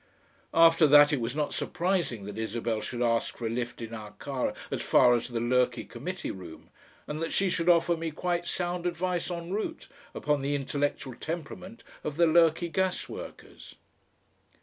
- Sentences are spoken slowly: No, average, 170 wpm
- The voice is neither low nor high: Yes, medium, 150 Hz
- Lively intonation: Yes, wide, 6.2 semitones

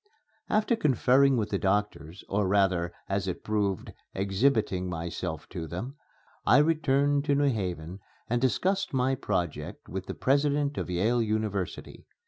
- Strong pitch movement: Yes, wide, 6.6 semitones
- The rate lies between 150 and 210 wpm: No, average, 140 wpm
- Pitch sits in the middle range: No, low, 110 Hz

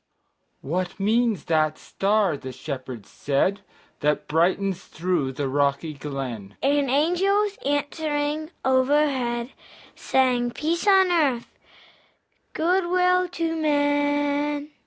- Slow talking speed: Yes, slow, 100 wpm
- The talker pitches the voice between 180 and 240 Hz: No, very high, 260 Hz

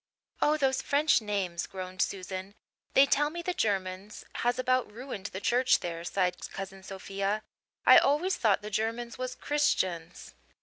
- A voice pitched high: Yes, high, 210 Hz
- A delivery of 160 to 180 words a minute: No, average, 150 wpm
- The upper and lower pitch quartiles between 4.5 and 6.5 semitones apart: Yes, average, 5.2 semitones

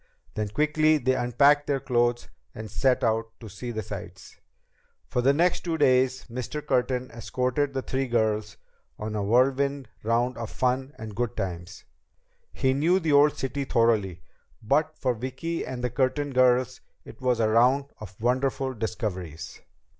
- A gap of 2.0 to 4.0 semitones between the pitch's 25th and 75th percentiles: Yes, average, 3.4 semitones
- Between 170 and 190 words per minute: No, average, 160 wpm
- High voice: No, low, 125 Hz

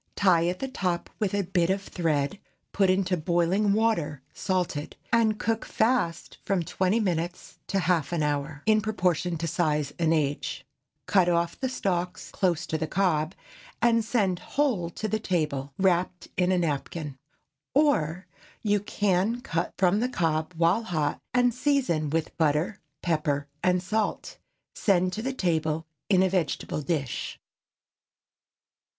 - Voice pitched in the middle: Yes, medium, 180 Hz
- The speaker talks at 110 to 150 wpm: Yes, average, 145 wpm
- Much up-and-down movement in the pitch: No, average, 4.1 semitones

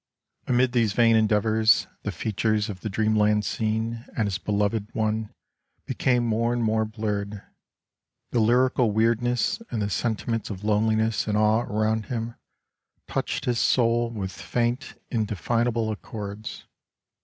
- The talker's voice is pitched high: No, low, 110 Hz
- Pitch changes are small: Yes, narrow, 1.7 semitones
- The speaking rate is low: Yes, slow, 130 wpm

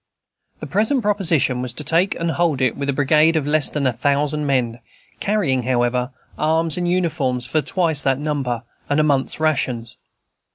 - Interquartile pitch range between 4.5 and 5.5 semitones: No, average, 3.9 semitones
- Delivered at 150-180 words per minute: Yes, average, 175 wpm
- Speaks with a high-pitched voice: No, medium, 145 Hz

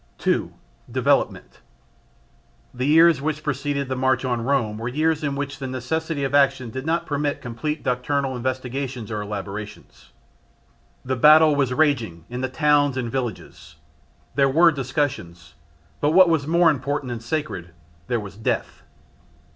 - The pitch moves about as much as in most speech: Yes, average, 3.6 semitones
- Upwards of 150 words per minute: No, average, 145 wpm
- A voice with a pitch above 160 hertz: No, low, 135 Hz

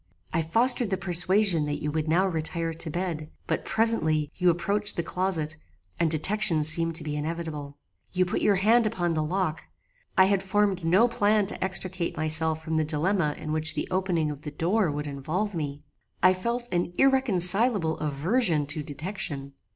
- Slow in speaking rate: No, average, 175 wpm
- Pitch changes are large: No, average, 3.9 semitones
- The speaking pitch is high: No, medium, 170 Hz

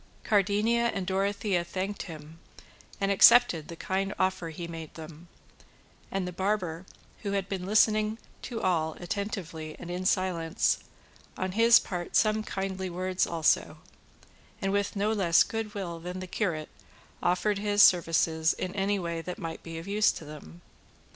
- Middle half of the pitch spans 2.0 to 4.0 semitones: Yes, average, 3.3 semitones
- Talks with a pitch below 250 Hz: Yes, medium, 185 Hz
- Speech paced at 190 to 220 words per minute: No, average, 155 wpm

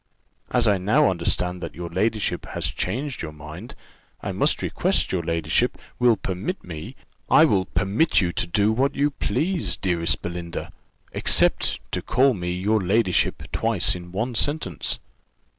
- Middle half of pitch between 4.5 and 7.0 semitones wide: Yes, average, 5.1 semitones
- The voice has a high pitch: No, very low, 95 Hz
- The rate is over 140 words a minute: Yes, average, 160 wpm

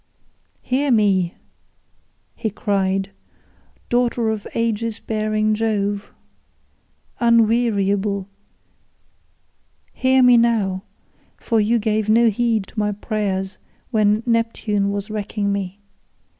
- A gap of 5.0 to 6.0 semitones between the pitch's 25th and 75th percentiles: No, narrow, 2.4 semitones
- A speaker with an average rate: No, slow, 95 wpm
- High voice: Yes, high, 215 Hz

